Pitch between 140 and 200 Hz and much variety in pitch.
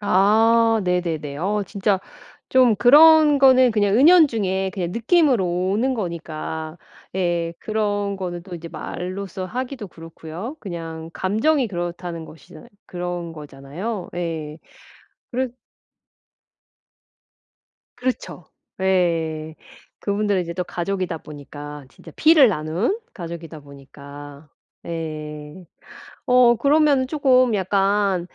Yes: medium, 185 Hz; wide, 5.7 semitones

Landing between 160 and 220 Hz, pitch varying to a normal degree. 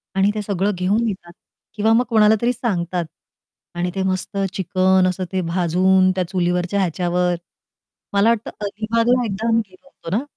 Yes: high, 190 Hz; average, 3.2 semitones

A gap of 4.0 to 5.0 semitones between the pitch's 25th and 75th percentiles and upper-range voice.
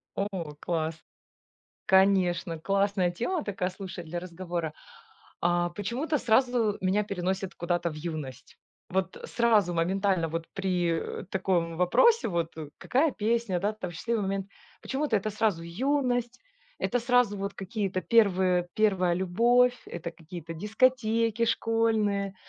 Yes: average, 4.5 semitones; high, 195 Hz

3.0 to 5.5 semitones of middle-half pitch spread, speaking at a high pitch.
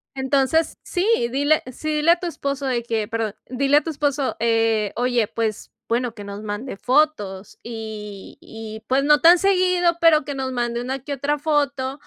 Yes: average, 4.7 semitones; very high, 265 Hz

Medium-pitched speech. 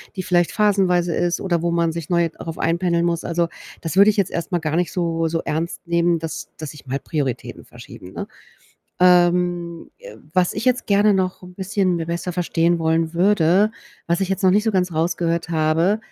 Yes: medium, 175 Hz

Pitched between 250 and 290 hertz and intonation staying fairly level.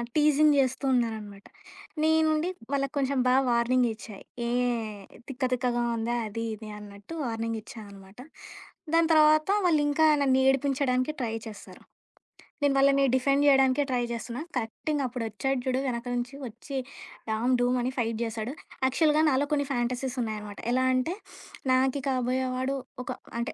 No: very high, 255 Hz; average, 3.1 semitones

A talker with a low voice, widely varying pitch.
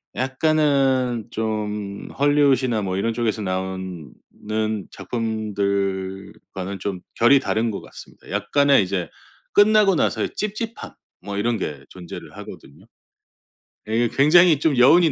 Yes: low, 110 Hz; wide, 6.2 semitones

